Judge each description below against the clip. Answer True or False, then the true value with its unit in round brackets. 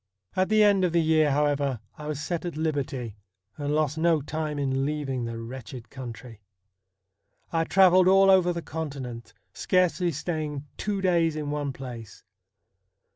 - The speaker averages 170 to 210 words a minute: False (155 wpm)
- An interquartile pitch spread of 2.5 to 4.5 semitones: True (4.2 semitones)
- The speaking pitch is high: False (150 Hz)